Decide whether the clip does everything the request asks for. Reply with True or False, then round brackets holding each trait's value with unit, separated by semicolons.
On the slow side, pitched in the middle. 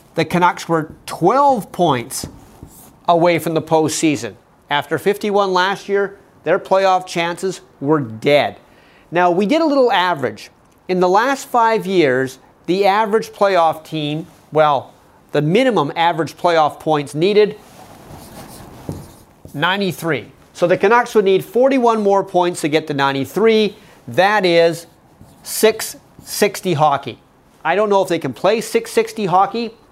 True (130 wpm; 180 Hz)